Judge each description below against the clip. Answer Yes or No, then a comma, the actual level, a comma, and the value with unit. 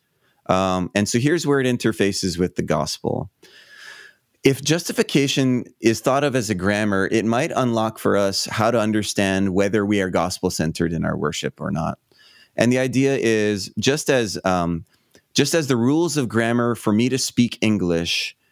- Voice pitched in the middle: No, low, 115 Hz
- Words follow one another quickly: No, average, 175 wpm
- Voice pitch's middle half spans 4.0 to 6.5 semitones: Yes, average, 4.9 semitones